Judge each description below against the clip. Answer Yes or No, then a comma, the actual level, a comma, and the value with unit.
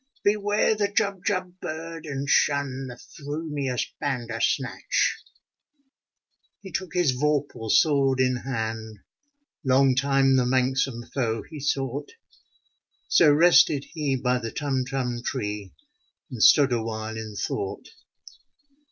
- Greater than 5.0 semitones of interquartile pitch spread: No, average, 3.7 semitones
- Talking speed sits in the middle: No, slow, 115 wpm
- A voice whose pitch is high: No, low, 135 Hz